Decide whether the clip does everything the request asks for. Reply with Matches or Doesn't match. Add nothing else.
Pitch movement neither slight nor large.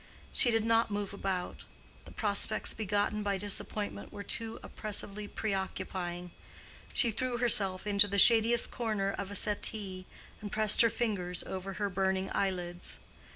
Doesn't match